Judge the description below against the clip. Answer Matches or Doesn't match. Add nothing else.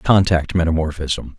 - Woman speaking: Doesn't match